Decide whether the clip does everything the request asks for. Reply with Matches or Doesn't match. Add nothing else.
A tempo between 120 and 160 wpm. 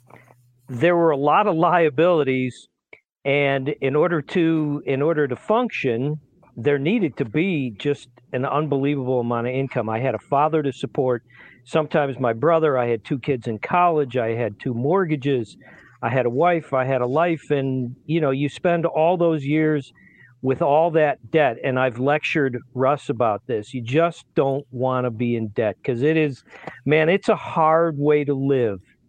Doesn't match